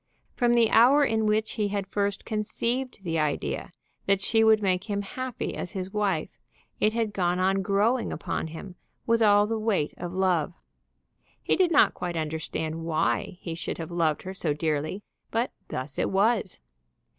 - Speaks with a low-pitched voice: No, high, 195 Hz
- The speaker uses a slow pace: No, average, 175 wpm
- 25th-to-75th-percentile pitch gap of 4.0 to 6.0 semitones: Yes, average, 4.5 semitones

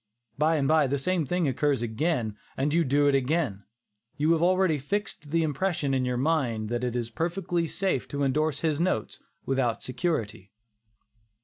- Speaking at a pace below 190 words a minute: Yes, average, 175 wpm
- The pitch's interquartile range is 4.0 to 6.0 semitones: Yes, average, 4.6 semitones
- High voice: No, medium, 145 Hz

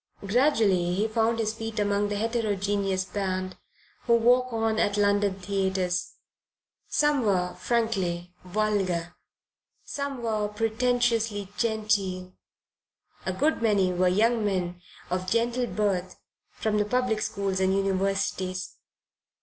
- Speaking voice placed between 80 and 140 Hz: No, high, 205 Hz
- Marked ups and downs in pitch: No, average, 3.2 semitones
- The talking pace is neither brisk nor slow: No, slow, 115 wpm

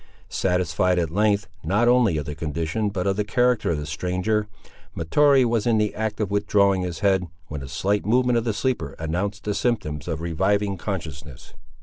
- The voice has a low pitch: Yes, low, 100 Hz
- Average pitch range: Yes, average, 4.5 semitones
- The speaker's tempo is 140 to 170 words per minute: No, average, 190 wpm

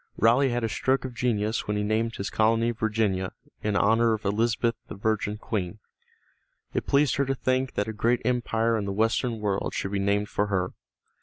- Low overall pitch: Yes, low, 110 Hz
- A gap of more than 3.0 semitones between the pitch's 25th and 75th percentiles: No, narrow, 2.4 semitones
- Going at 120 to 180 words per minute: No, average, 200 wpm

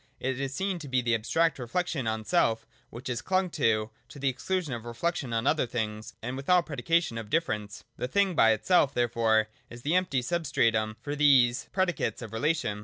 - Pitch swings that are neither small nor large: No, wide, 6.4 semitones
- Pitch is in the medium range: No, low, 130 Hz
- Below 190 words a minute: No, average, 195 wpm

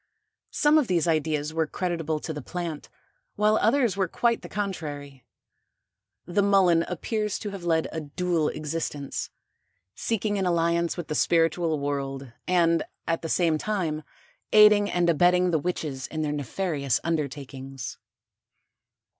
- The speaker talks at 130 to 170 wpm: Yes, average, 140 wpm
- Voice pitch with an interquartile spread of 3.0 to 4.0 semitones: Yes, average, 3.6 semitones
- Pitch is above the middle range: No, medium, 165 Hz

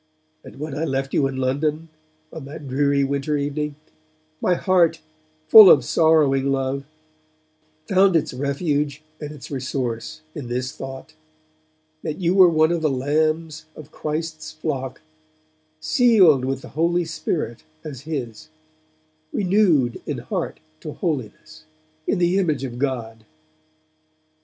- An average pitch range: Yes, average, 3.1 semitones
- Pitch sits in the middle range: Yes, medium, 150 Hz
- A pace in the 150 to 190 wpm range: No, slow, 135 wpm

